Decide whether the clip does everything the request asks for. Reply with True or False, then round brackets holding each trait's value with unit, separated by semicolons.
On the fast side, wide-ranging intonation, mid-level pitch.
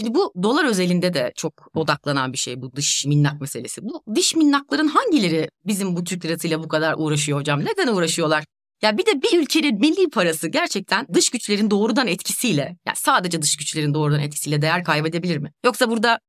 True (190 wpm; 7.4 semitones; 175 Hz)